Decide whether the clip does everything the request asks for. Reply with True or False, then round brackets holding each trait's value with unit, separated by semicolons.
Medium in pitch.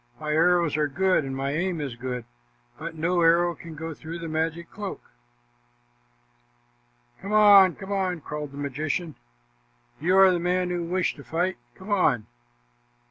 True (170 Hz)